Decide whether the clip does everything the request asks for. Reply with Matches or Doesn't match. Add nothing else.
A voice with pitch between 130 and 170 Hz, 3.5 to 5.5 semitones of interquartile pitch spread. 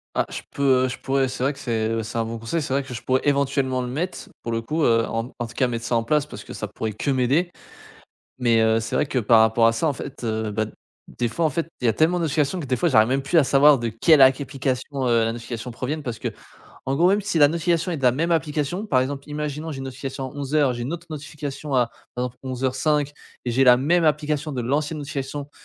Matches